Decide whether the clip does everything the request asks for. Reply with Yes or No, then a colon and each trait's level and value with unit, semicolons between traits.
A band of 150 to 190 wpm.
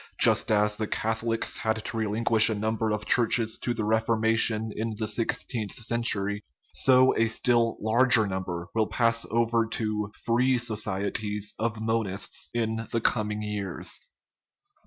Yes: average, 155 wpm